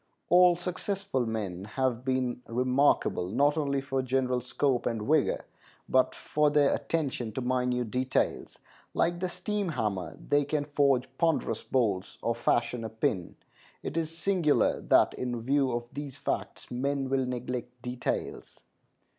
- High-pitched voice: No, low, 130 Hz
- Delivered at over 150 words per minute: No, average, 145 wpm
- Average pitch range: Yes, average, 3.1 semitones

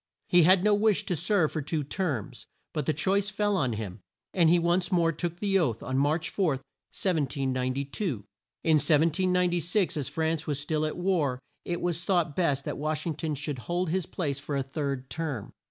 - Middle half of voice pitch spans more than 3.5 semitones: Yes, average, 4.1 semitones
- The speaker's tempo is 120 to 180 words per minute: No, average, 190 wpm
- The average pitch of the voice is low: No, medium, 160 Hz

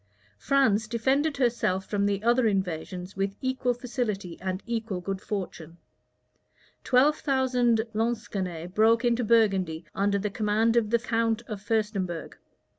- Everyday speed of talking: No, slow, 130 wpm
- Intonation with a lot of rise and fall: No, average, 3.6 semitones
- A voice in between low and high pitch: No, high, 215 Hz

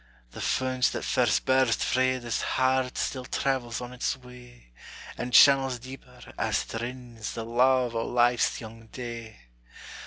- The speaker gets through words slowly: No, average, 150 wpm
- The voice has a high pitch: No, low, 125 Hz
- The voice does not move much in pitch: Yes, narrow, 1.7 semitones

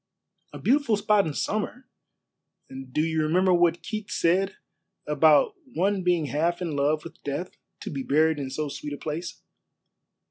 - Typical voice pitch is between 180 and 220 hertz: No, medium, 170 Hz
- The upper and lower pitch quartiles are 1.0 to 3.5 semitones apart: No, average, 4.3 semitones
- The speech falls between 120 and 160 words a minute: Yes, average, 155 wpm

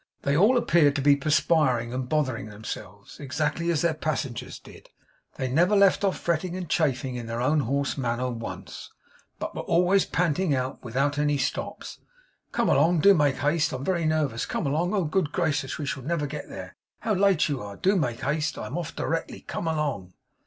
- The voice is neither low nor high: Yes, medium, 150 Hz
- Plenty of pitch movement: No, average, 4.4 semitones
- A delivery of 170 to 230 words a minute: Yes, average, 190 wpm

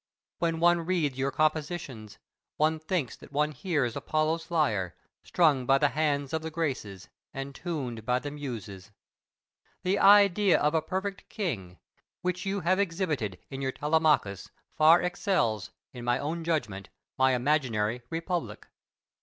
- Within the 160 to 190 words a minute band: No, average, 145 wpm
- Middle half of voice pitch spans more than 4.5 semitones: Yes, average, 5.3 semitones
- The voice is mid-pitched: Yes, medium, 150 Hz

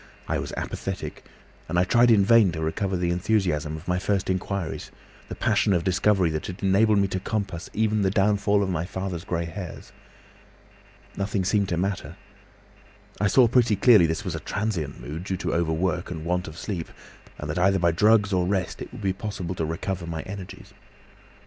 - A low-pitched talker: Yes, very low, 95 Hz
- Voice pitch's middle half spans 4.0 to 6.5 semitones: No, average, 2.9 semitones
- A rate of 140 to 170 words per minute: No, average, 195 wpm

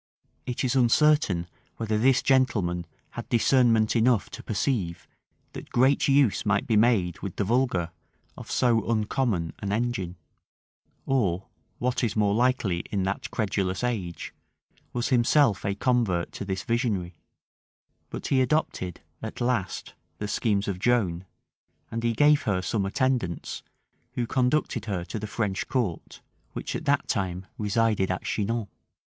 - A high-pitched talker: No, low, 110 Hz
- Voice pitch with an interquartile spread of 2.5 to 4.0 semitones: No, average, 4.4 semitones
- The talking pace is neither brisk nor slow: Yes, average, 145 wpm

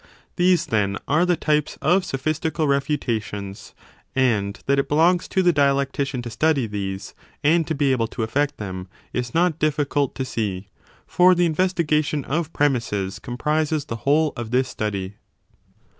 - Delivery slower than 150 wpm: No, average, 160 wpm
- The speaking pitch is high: No, medium, 140 Hz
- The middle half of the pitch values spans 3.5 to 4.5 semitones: No, wide, 5.5 semitones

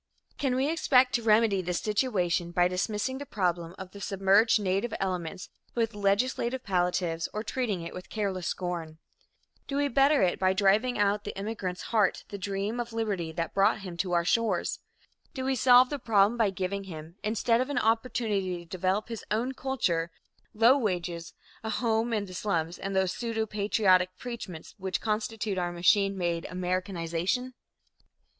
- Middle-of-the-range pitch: No, high, 200 Hz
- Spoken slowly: No, average, 170 wpm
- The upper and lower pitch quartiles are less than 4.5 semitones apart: Yes, average, 4.1 semitones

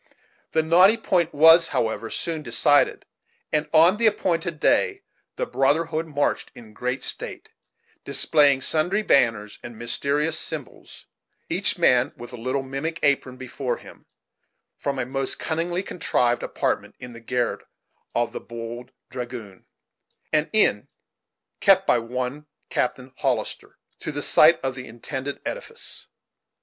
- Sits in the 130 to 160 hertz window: Yes, medium, 140 Hz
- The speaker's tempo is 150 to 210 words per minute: No, slow, 135 wpm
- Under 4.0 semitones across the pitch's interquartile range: No, average, 5.0 semitones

